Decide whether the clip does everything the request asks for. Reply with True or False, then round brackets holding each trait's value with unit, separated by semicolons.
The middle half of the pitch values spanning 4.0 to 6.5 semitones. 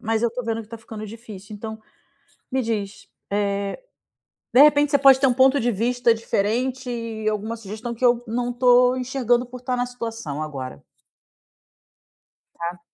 False (2.4 semitones)